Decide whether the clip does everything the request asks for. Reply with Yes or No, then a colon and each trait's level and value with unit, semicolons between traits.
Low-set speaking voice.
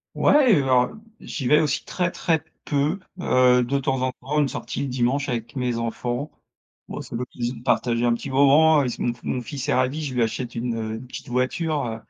Yes: low, 130 Hz